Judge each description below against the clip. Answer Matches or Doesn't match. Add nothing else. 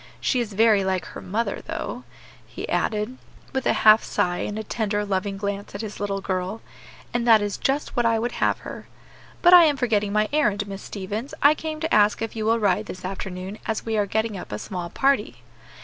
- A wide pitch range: Doesn't match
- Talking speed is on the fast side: Matches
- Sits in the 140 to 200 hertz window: Doesn't match